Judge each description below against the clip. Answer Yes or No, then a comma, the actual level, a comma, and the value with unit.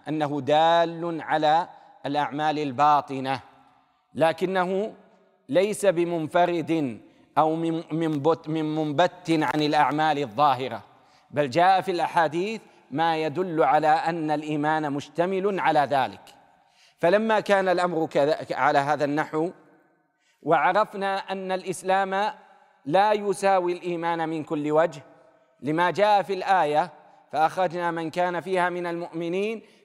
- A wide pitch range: No, average, 3.1 semitones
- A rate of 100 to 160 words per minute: Yes, average, 110 wpm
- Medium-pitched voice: Yes, medium, 165 Hz